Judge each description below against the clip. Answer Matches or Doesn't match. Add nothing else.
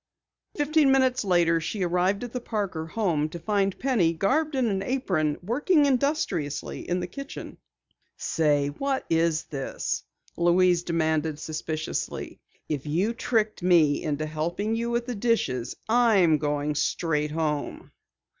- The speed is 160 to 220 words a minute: Doesn't match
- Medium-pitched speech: Matches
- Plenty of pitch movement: Matches